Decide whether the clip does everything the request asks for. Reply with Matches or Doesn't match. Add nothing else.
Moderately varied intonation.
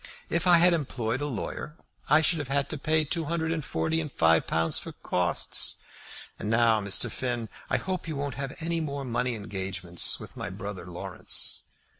Doesn't match